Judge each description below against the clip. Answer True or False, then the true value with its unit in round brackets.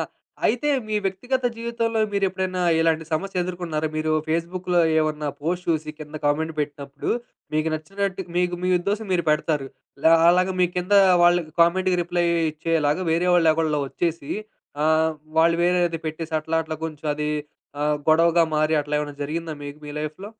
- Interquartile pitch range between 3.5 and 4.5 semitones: False (2.7 semitones)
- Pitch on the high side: False (165 Hz)